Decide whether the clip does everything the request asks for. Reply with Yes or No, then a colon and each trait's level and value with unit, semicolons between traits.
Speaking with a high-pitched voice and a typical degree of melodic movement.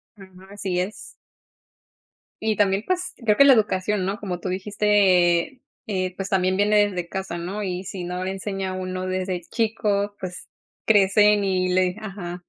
No: high, 195 Hz; narrow, 2.1 semitones